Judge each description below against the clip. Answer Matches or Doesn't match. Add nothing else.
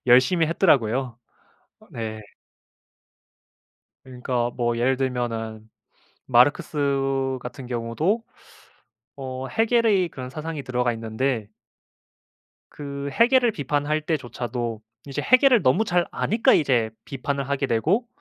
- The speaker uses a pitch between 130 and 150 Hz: Matches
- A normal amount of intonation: Matches